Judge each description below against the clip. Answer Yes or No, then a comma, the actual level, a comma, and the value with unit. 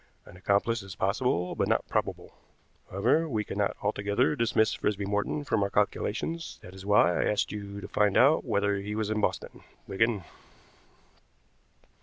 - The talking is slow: No, average, 160 wpm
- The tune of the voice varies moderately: No, narrow, 2.1 semitones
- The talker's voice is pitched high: No, low, 105 Hz